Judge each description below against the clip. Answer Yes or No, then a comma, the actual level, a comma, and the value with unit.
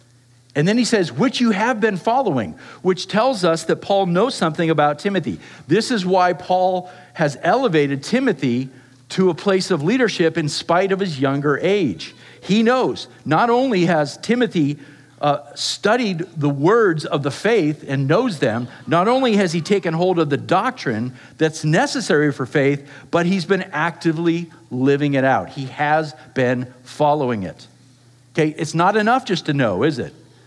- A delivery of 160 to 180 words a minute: Yes, average, 170 wpm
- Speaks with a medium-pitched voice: Yes, medium, 165 Hz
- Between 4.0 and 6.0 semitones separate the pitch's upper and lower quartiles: Yes, average, 5.1 semitones